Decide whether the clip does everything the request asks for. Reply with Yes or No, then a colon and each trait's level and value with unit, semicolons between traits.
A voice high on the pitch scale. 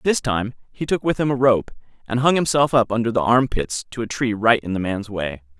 No: low, 115 Hz